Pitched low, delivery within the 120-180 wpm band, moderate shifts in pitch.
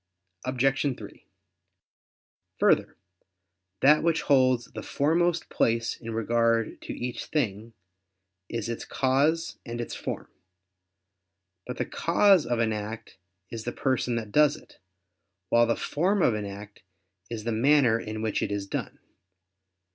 Yes: low, 120 Hz; average, 140 wpm; average, 4.1 semitones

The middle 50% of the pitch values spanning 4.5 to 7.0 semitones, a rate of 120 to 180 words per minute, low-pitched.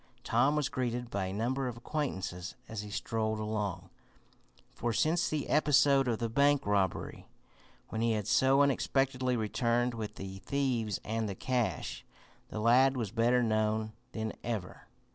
No: average, 3.5 semitones; average, 155 wpm; low, 115 Hz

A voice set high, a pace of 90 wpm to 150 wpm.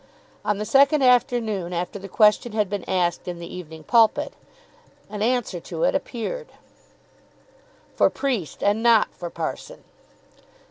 Yes: high, 210 Hz; average, 140 wpm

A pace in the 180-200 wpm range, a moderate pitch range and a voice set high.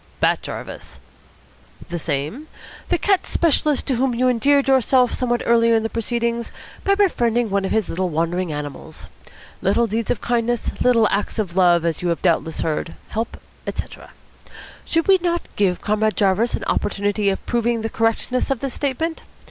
No: average, 165 wpm; average, 4.7 semitones; high, 230 Hz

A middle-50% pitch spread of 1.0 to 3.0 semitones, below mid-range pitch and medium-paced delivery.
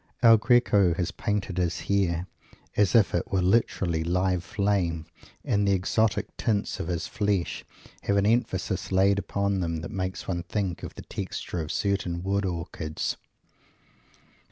Yes: narrow, 2.6 semitones; very low, 95 Hz; average, 155 wpm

